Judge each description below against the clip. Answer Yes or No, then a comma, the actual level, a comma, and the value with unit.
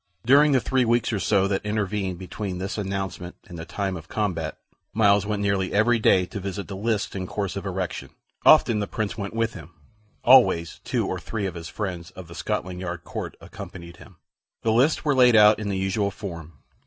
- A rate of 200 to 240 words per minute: Yes, fast, 205 wpm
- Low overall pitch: Yes, low, 100 Hz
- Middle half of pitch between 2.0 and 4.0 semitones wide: Yes, average, 2.9 semitones